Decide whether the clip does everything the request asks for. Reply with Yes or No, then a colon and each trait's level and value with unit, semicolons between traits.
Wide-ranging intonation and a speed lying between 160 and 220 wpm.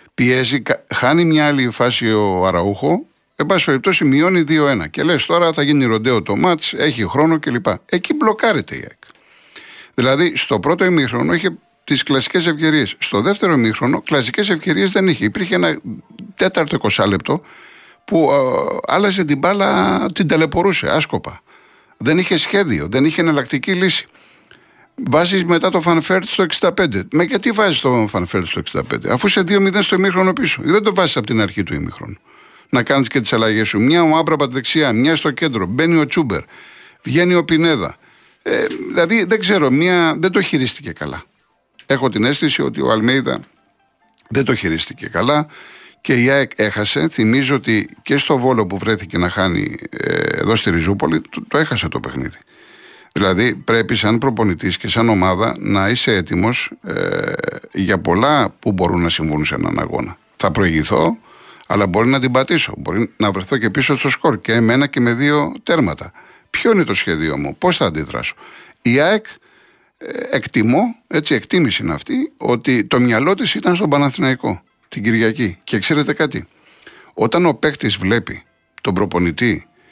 Yes: wide, 7.7 semitones; average, 165 wpm